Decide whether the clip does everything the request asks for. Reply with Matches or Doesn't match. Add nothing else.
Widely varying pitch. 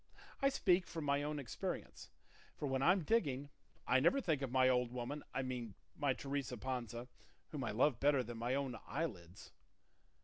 Doesn't match